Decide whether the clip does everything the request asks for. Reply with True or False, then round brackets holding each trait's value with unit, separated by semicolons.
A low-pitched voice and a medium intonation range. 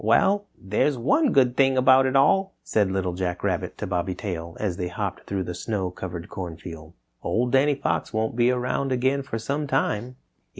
False (115 Hz; 6.6 semitones)